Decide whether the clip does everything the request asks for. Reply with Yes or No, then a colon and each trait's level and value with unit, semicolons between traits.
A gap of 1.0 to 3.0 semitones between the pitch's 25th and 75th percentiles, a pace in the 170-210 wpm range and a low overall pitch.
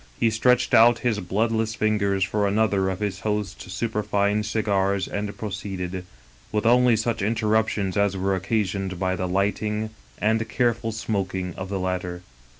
No: narrow, 2.6 semitones; average, 150 wpm; low, 105 Hz